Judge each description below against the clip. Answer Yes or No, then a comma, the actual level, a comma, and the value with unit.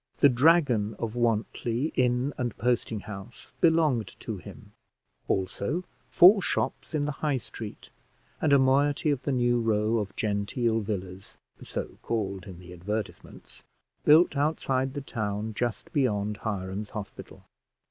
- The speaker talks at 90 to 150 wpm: Yes, slow, 135 wpm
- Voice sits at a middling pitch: No, low, 115 Hz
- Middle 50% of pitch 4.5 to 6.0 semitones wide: Yes, average, 5.1 semitones